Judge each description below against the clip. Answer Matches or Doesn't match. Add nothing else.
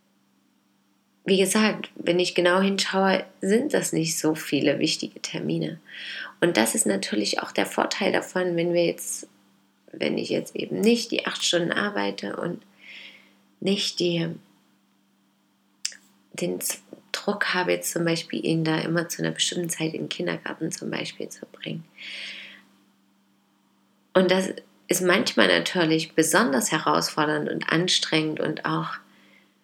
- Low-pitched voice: Doesn't match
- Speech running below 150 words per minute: Matches